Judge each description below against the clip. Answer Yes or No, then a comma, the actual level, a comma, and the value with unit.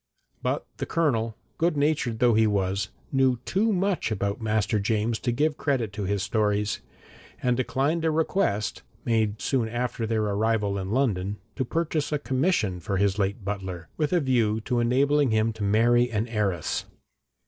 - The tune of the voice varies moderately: Yes, average, 4.6 semitones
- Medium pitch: No, low, 115 Hz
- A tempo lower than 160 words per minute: No, average, 170 wpm